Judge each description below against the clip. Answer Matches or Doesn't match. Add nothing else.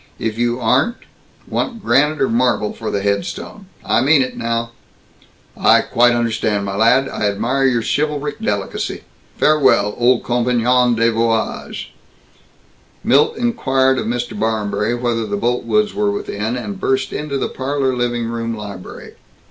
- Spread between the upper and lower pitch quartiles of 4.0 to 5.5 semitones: Doesn't match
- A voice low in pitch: Matches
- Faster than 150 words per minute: Doesn't match